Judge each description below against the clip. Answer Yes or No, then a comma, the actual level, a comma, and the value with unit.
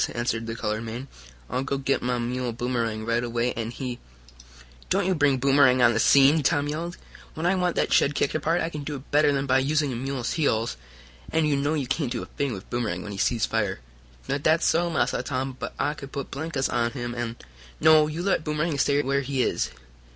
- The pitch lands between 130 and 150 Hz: Yes, low, 135 Hz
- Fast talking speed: Yes, fast, 230 wpm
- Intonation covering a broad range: No, average, 3.8 semitones